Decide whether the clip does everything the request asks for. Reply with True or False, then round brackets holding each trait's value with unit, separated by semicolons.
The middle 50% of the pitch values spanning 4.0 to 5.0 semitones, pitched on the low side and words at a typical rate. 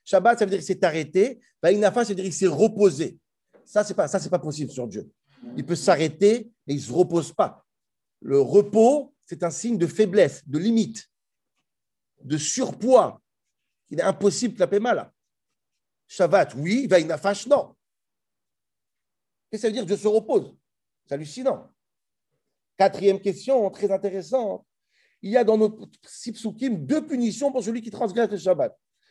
False (4.3 semitones; 205 Hz; 165 wpm)